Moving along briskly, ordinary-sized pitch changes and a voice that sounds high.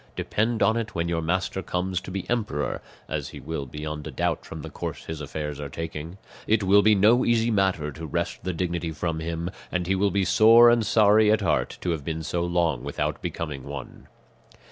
No: fast, 210 wpm; average, 4.4 semitones; very low, 85 Hz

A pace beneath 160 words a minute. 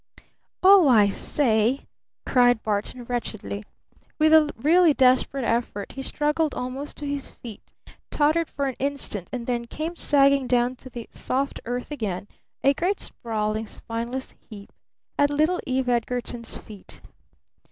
Yes: average, 140 wpm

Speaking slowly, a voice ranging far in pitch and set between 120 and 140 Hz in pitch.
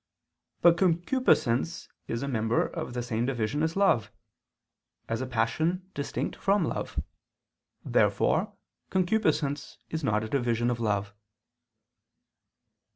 Yes: slow, 115 wpm; wide, 6.7 semitones; low, 135 Hz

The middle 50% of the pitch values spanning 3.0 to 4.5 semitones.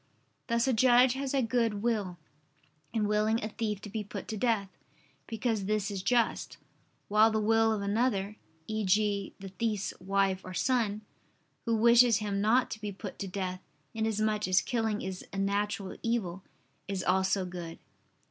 No: narrow, 2.5 semitones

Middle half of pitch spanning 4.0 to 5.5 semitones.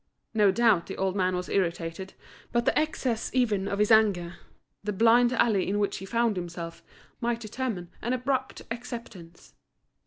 Yes: average, 4.3 semitones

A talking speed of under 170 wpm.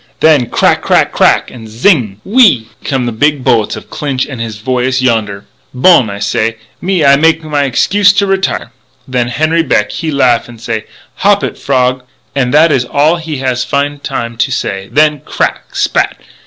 No: average, 190 wpm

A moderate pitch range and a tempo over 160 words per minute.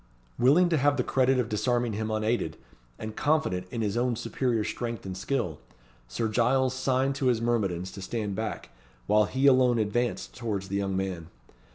Yes: average, 4.0 semitones; average, 180 wpm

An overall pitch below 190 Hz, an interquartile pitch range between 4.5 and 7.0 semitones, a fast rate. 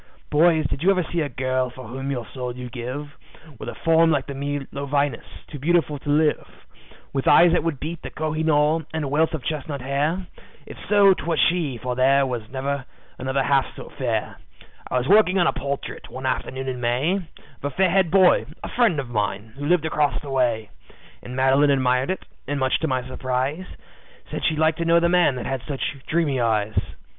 No: medium, 140 Hz; average, 3.8 semitones; fast, 210 wpm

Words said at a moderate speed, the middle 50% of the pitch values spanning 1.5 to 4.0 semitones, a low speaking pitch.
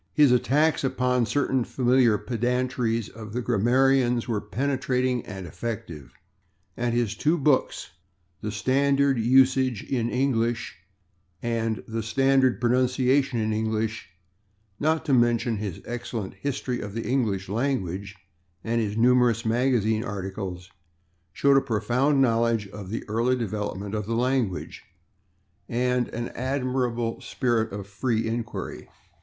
No: slow, 130 wpm; average, 2.8 semitones; low, 120 Hz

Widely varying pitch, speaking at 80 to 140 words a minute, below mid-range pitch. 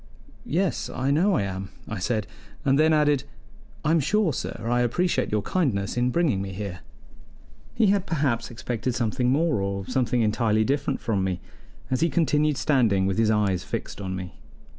No: wide, 6.8 semitones; average, 175 wpm; low, 125 Hz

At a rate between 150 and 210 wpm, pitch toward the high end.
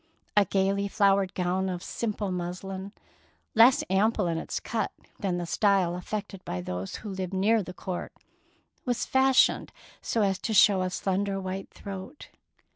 Yes: average, 155 wpm; high, 195 Hz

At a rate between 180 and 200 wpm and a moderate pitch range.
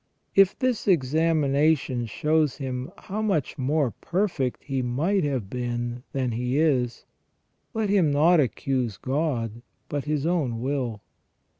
No: slow, 135 wpm; average, 4.4 semitones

